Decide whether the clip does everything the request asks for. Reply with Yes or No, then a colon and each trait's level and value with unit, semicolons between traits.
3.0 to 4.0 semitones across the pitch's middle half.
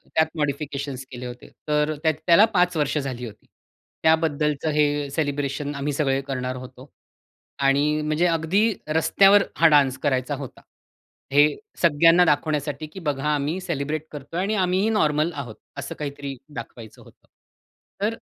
No: narrow, 2.6 semitones